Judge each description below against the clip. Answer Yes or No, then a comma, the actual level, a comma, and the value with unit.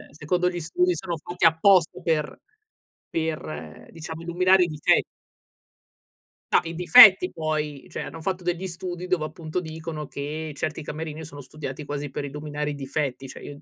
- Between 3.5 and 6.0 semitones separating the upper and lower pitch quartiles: No, average, 2.9 semitones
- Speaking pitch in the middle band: Yes, medium, 160 Hz